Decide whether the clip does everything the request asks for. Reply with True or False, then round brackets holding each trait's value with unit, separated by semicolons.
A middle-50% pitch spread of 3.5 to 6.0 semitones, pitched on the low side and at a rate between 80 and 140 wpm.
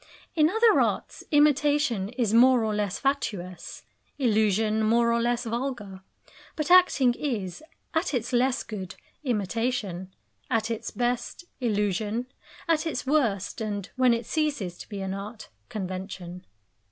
False (4.4 semitones; 230 Hz; 135 wpm)